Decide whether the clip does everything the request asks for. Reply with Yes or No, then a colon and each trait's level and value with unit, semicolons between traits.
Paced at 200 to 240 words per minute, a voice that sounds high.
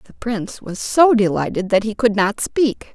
Yes: fast, 205 wpm; high, 215 Hz